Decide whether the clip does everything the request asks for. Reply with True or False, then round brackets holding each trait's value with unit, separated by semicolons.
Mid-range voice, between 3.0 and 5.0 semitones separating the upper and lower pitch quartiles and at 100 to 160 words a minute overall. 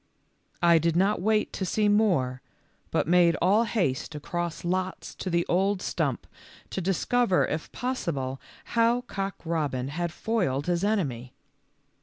True (175 Hz; 4.5 semitones; 140 wpm)